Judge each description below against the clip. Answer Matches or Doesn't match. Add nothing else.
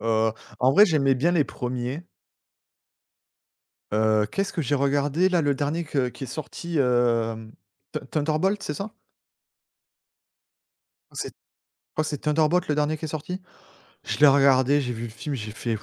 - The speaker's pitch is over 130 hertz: Matches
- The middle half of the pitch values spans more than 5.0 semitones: Doesn't match